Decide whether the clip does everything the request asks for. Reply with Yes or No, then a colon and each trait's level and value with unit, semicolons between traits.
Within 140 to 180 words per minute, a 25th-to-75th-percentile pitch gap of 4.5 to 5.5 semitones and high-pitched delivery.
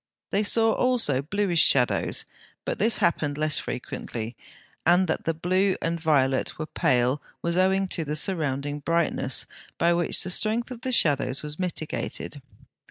No: average, 155 wpm; average, 4.8 semitones; medium, 165 Hz